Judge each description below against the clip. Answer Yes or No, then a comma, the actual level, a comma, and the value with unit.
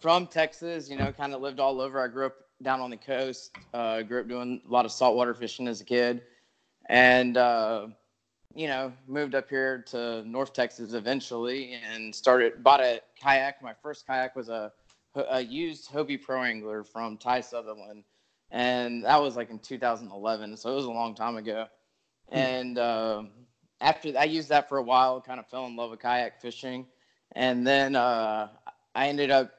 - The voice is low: Yes, low, 125 Hz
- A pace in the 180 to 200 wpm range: Yes, average, 190 wpm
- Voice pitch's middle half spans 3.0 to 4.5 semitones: No, narrow, 2.6 semitones